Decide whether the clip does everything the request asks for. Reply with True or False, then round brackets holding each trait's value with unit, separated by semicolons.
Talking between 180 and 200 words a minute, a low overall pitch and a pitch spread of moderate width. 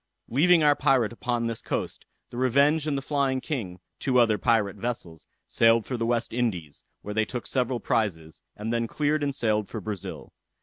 True (185 wpm; 120 Hz; 4.0 semitones)